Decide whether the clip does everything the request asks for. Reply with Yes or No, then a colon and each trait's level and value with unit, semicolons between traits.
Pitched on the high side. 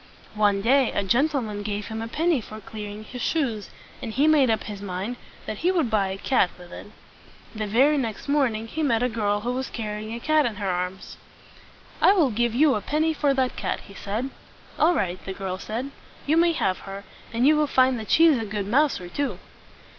Yes: high, 230 Hz